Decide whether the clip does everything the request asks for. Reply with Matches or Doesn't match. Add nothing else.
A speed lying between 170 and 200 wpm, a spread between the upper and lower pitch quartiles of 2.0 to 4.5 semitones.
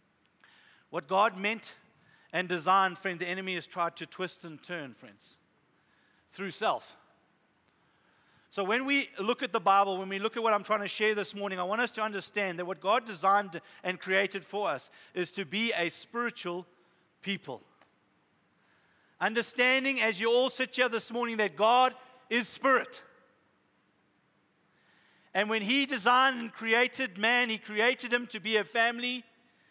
Doesn't match